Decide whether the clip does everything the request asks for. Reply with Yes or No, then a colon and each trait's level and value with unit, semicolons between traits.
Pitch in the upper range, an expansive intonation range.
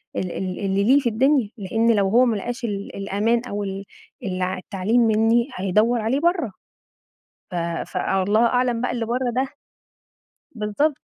No: high, 225 Hz; average, 3.7 semitones